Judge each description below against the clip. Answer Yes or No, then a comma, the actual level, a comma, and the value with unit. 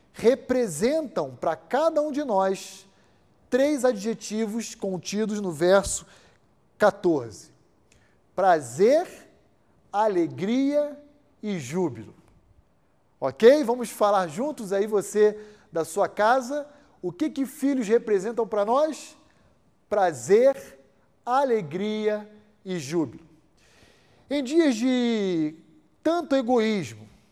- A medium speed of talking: No, slow, 90 wpm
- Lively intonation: Yes, wide, 6.0 semitones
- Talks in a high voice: Yes, high, 215 Hz